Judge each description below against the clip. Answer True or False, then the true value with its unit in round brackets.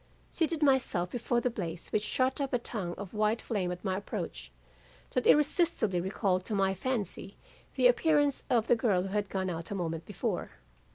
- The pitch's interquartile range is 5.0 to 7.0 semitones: True (5.4 semitones)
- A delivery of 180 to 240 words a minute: True (185 wpm)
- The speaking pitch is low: False (210 Hz)